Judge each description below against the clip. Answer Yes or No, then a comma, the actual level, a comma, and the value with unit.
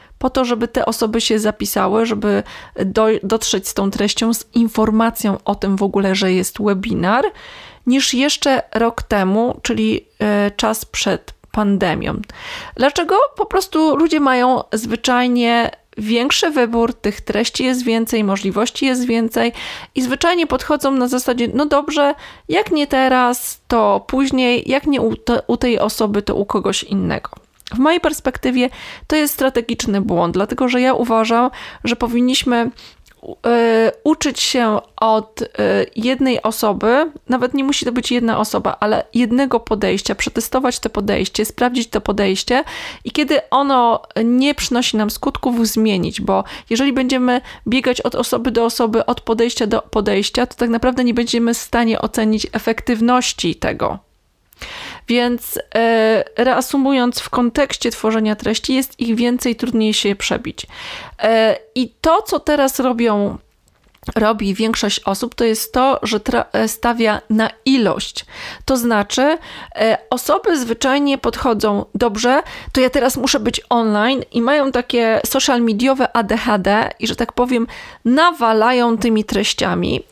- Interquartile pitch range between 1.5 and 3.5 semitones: Yes, average, 2.9 semitones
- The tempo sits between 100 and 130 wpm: No, average, 140 wpm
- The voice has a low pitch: No, high, 240 Hz